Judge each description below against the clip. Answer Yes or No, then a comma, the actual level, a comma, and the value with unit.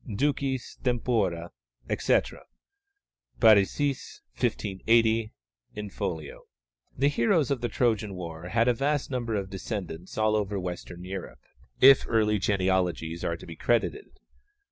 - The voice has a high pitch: No, low, 105 Hz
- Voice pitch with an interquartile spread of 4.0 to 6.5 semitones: Yes, average, 4.7 semitones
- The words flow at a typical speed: No, slow, 120 wpm